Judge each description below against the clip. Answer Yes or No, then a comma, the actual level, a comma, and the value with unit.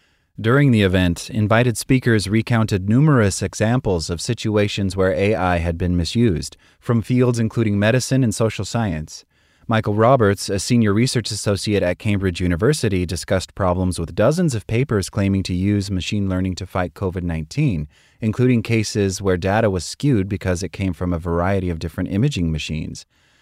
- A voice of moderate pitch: No, low, 100 Hz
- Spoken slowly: No, average, 160 wpm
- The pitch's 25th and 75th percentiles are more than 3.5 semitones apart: Yes, average, 3.9 semitones